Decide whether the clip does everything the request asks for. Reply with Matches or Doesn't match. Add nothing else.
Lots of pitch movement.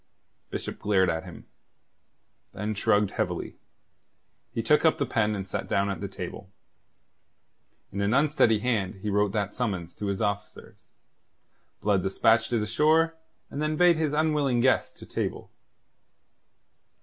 Matches